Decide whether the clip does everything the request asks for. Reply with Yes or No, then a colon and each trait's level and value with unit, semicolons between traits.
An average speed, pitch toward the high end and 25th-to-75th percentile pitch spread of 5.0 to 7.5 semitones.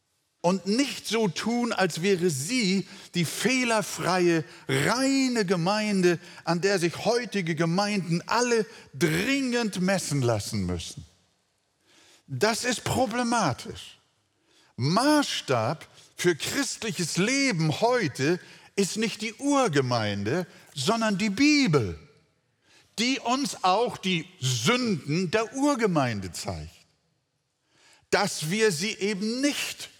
No: slow, 100 wpm; high, 195 Hz; wide, 5.5 semitones